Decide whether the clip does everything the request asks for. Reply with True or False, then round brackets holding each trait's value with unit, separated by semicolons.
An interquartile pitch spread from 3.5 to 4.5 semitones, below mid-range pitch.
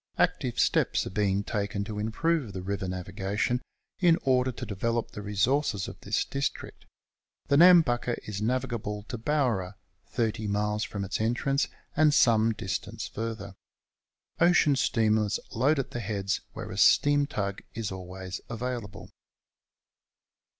True (4.2 semitones; 110 Hz)